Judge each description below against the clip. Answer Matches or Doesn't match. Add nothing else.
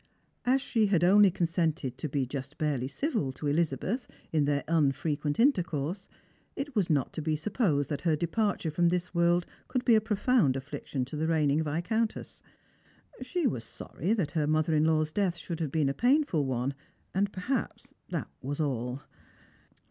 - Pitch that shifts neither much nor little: Doesn't match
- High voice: Doesn't match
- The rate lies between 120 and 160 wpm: Doesn't match